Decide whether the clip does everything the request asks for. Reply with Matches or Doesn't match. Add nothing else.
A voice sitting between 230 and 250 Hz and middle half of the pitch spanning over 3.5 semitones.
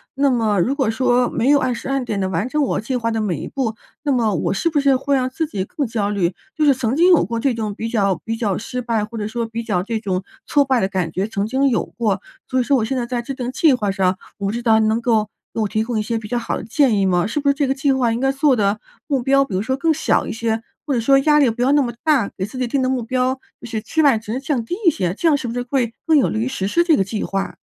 Matches